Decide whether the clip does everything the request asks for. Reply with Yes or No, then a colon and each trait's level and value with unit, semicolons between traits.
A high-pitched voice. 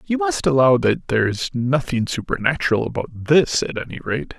No: low, 125 Hz